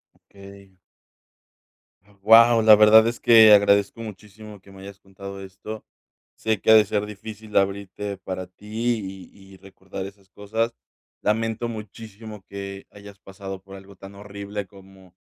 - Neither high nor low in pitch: No, low, 100 Hz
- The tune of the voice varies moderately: No, narrow, 1.9 semitones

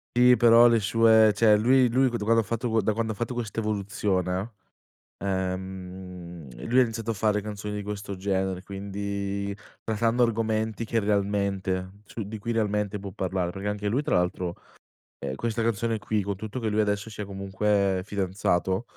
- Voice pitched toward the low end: Yes, low, 105 Hz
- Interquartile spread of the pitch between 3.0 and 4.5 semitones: No, narrow, 2.6 semitones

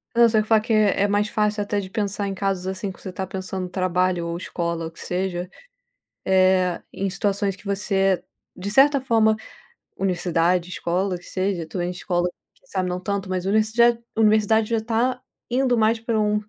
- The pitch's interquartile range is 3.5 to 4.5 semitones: No, average, 2.9 semitones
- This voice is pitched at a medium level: No, high, 195 Hz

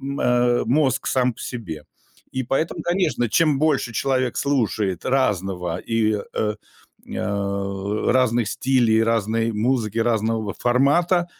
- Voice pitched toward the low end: Yes, low, 115 Hz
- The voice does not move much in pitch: No, average, 4.0 semitones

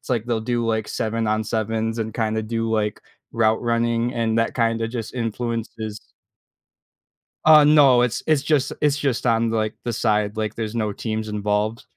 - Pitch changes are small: Yes, narrow, 1.4 semitones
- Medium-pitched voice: No, low, 115 Hz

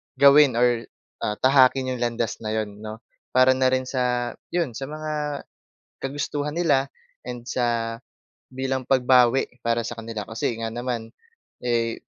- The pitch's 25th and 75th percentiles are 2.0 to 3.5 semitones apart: Yes, narrow, 2.5 semitones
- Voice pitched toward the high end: No, low, 125 Hz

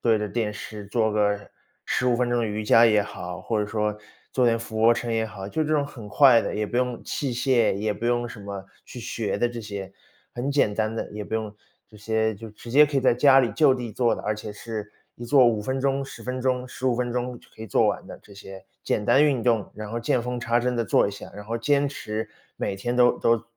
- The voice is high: No, low, 115 Hz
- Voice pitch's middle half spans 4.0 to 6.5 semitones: No, average, 2.9 semitones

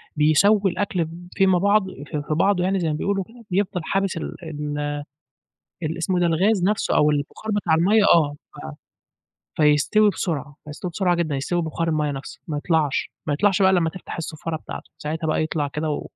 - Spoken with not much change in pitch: No, average, 4.0 semitones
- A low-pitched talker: No, medium, 165 Hz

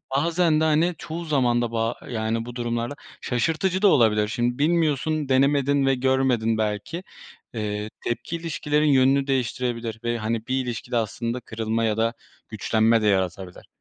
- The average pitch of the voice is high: No, low, 120 Hz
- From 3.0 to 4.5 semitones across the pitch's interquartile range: Yes, average, 4.2 semitones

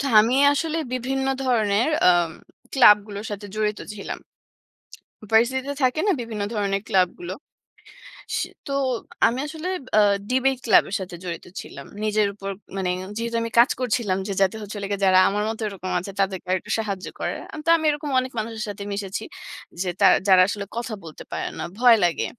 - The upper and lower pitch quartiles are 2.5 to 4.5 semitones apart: Yes, average, 3.9 semitones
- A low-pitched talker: No, high, 210 Hz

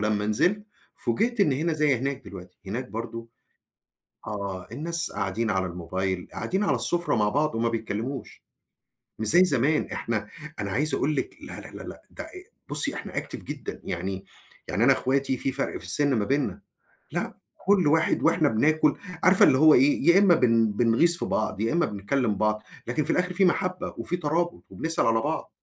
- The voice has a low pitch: Yes, low, 130 Hz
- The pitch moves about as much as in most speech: No, wide, 6.9 semitones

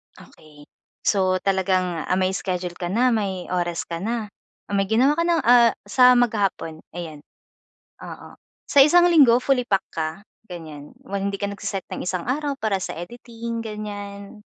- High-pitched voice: Yes, high, 200 Hz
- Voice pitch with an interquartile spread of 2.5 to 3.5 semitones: No, average, 4.6 semitones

